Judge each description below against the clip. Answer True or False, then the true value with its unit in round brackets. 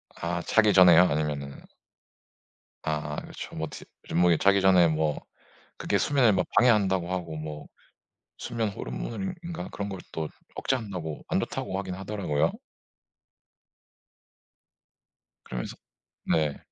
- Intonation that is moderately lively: True (4.7 semitones)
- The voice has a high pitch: False (90 Hz)